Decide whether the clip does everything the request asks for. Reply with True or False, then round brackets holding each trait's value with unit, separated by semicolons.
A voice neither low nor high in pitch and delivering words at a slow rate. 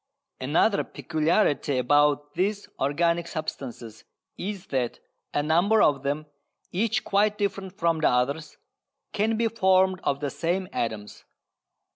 True (165 Hz; 125 wpm)